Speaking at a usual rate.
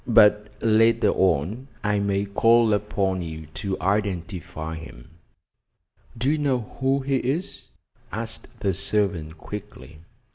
No: slow, 120 wpm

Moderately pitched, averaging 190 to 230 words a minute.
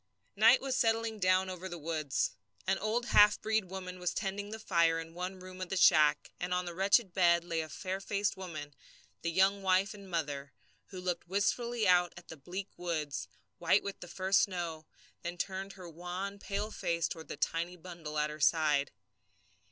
Yes: medium, 180 Hz; average, 195 wpm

